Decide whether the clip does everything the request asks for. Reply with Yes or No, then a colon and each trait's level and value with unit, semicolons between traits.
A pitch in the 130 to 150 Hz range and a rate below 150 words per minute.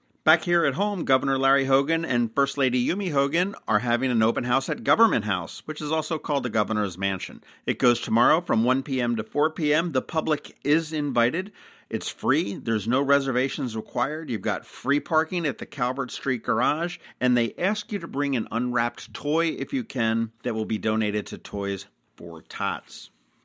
No: low, 135 Hz; average, 190 wpm